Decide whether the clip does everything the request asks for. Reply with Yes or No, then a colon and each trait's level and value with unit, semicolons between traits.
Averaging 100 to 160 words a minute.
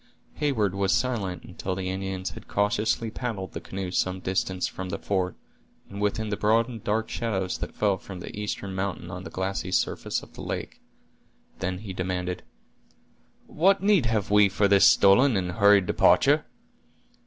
No: average, 170 wpm